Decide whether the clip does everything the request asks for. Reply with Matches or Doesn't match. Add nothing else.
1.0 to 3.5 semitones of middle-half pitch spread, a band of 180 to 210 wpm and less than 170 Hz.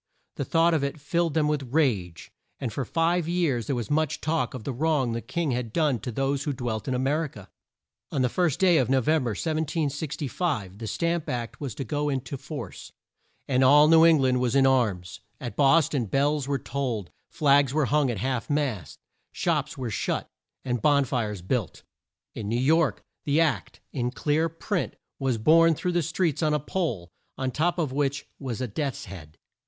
Doesn't match